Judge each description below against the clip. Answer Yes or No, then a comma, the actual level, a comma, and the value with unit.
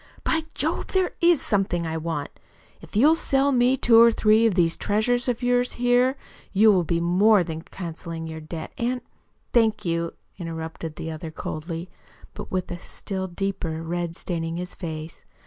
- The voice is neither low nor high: Yes, medium, 180 Hz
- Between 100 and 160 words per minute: No, average, 175 wpm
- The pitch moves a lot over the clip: Yes, wide, 6.1 semitones